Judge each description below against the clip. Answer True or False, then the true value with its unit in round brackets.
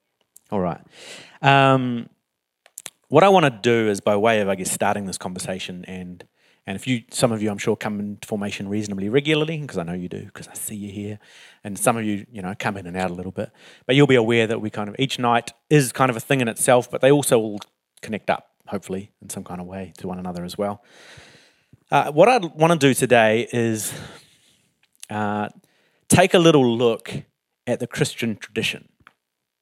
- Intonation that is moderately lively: True (4.7 semitones)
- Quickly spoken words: True (215 wpm)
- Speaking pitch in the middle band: False (110 Hz)